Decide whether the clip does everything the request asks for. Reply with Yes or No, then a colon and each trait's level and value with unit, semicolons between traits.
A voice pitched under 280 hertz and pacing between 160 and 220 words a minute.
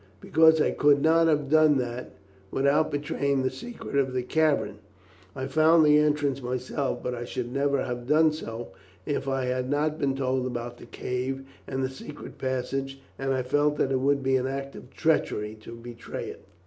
Yes: low, 135 Hz; average, 190 wpm